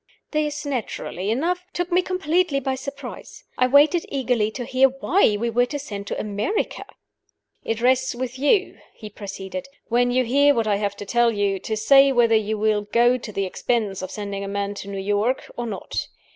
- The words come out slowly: No, average, 195 wpm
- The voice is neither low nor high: No, high, 240 Hz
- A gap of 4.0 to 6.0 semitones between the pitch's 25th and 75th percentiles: Yes, average, 5.0 semitones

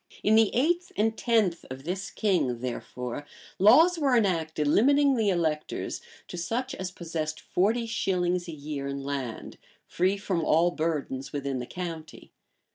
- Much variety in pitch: Yes, wide, 6.4 semitones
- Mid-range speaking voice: Yes, medium, 175 Hz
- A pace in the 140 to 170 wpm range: Yes, average, 150 wpm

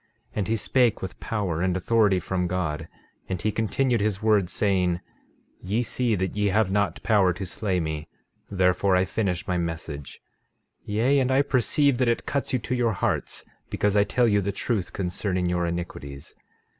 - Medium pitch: No, low, 100 Hz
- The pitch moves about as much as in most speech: Yes, average, 3.8 semitones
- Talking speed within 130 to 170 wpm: No, average, 185 wpm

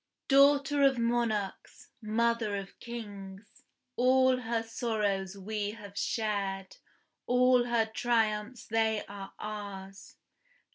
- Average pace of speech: No, slow, 100 wpm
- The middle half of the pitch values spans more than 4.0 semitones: No, average, 3.0 semitones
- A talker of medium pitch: No, high, 220 Hz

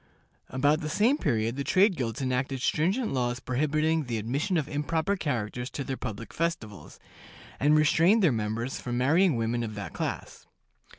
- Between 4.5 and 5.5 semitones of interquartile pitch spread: Yes, average, 5.1 semitones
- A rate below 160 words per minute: No, average, 165 wpm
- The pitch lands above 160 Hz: No, low, 135 Hz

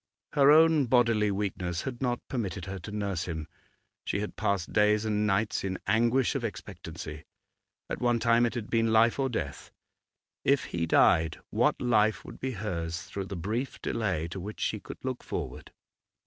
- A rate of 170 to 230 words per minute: Yes, average, 175 wpm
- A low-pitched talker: Yes, low, 105 Hz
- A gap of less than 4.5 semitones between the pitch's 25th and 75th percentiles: Yes, average, 4.1 semitones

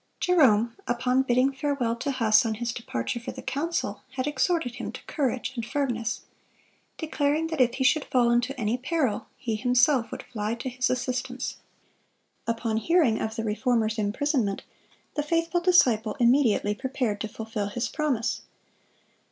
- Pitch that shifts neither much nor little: Yes, average, 3.7 semitones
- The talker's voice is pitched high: Yes, high, 245 Hz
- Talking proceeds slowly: No, average, 155 wpm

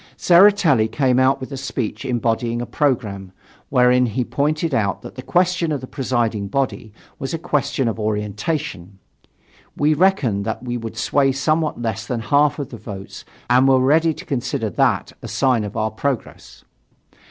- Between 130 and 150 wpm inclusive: No, average, 170 wpm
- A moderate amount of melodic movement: Yes, average, 4.5 semitones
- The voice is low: Yes, low, 130 Hz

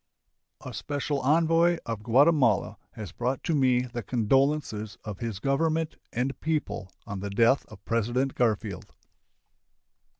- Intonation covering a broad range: No, average, 5.0 semitones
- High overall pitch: No, low, 125 Hz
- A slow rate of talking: Yes, slow, 130 wpm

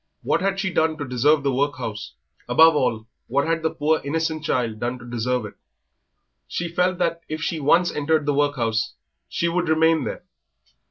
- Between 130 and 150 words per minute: No, average, 180 wpm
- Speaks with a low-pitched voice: No, medium, 150 Hz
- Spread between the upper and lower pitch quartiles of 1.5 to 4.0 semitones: No, average, 4.4 semitones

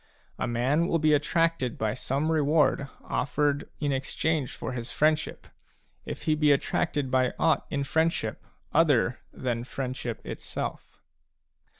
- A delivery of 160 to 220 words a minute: No, slow, 135 wpm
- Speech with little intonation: No, average, 3.4 semitones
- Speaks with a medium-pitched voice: Yes, medium, 145 Hz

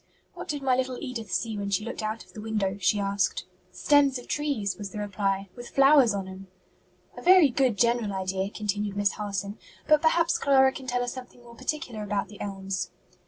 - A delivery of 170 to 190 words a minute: No, fast, 205 wpm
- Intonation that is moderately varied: Yes, average, 4.7 semitones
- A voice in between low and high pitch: No, high, 220 Hz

